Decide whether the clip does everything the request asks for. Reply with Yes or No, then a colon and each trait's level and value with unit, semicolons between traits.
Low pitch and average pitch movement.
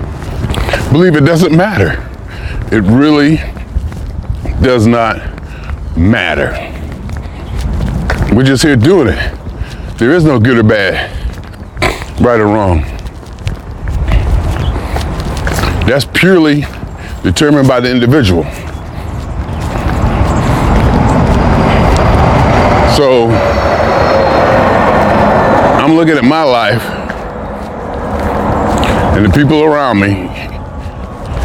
No: very low, 95 Hz; wide, 7.2 semitones